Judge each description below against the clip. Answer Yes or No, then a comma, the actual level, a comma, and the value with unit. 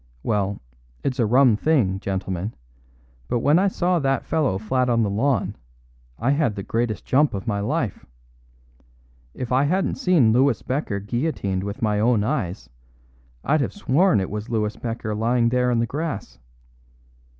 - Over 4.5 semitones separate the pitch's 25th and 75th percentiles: Yes, average, 5.1 semitones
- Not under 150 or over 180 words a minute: Yes, average, 160 wpm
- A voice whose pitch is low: Yes, low, 120 Hz